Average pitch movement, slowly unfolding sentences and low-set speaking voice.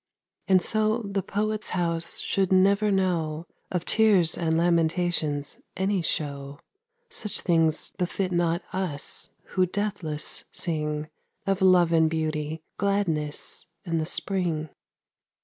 No: average, 3.4 semitones; slow, 115 wpm; medium, 175 Hz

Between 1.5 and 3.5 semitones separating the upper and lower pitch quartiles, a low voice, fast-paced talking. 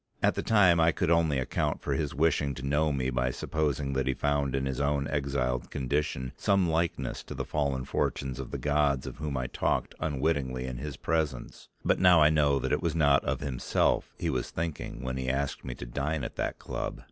Yes: average, 2.8 semitones; very low, 70 Hz; fast, 215 wpm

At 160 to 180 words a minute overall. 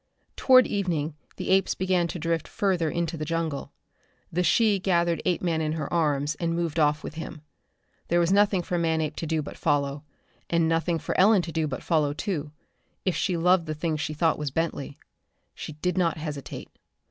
No: average, 190 wpm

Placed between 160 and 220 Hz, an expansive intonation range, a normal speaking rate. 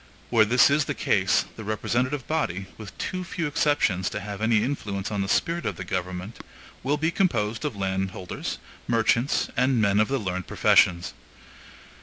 No: low, 110 Hz; wide, 6.0 semitones; average, 170 wpm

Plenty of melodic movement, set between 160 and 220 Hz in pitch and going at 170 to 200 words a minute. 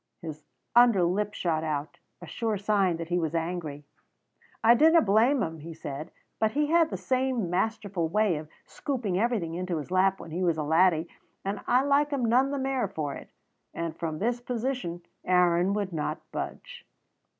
Yes: wide, 6.4 semitones; medium, 185 Hz; average, 185 wpm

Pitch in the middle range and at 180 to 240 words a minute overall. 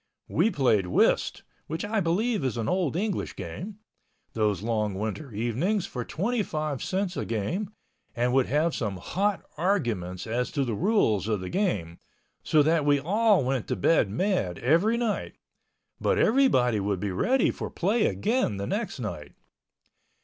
No: medium, 145 Hz; average, 155 wpm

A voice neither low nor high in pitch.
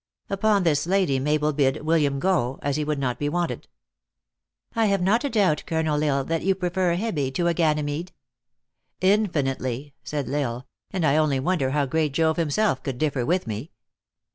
Yes: medium, 155 Hz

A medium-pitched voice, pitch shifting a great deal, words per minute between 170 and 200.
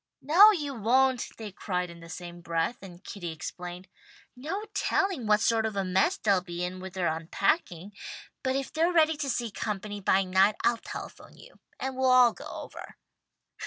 No: high, 210 Hz; wide, 6.5 semitones; average, 190 wpm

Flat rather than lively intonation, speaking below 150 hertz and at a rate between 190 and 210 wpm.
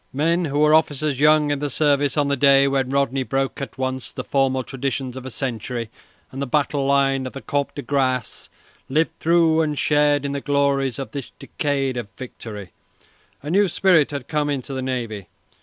Yes: narrow, 2.0 semitones; medium, 140 Hz; average, 195 wpm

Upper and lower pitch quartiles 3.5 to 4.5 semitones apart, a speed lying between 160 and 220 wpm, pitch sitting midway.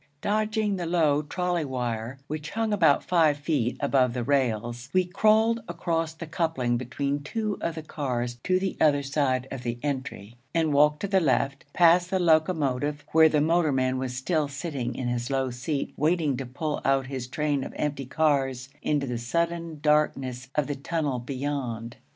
Yes: average, 4.2 semitones; average, 175 wpm; medium, 145 Hz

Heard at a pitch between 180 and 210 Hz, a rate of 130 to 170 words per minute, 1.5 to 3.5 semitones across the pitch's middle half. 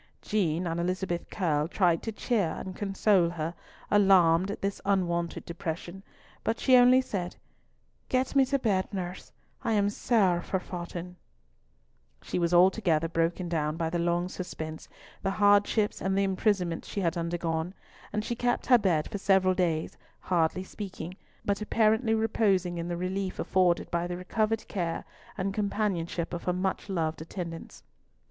Yes: medium, 185 Hz; average, 155 wpm; average, 3.0 semitones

